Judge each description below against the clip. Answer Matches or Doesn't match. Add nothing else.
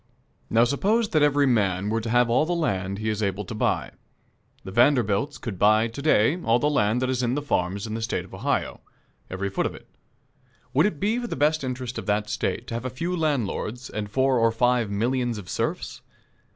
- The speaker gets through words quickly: Matches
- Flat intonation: Doesn't match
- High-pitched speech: Doesn't match